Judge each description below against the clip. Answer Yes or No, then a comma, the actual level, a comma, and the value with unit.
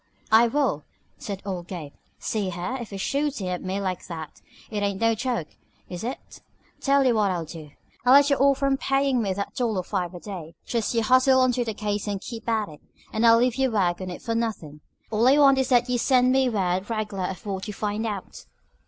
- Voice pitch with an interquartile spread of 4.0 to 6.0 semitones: Yes, average, 5.0 semitones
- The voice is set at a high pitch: Yes, high, 215 Hz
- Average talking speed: No, fast, 230 wpm